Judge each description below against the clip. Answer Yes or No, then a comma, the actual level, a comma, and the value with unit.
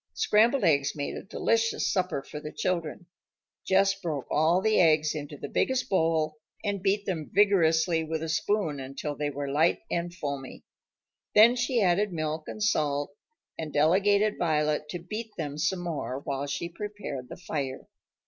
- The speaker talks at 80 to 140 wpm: No, average, 165 wpm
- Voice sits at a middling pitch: Yes, medium, 165 Hz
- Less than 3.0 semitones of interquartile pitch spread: No, average, 4.8 semitones